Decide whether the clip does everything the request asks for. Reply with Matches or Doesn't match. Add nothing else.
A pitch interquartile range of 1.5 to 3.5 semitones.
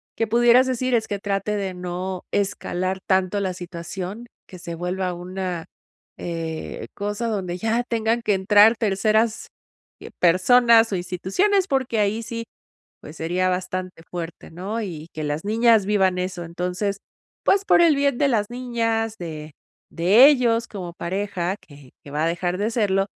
Doesn't match